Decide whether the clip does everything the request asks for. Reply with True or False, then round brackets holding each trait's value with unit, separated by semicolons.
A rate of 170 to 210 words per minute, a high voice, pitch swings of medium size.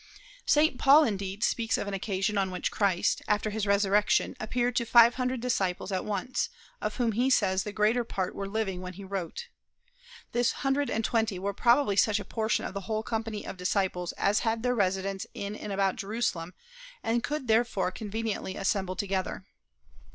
True (180 wpm; 210 Hz; 3.1 semitones)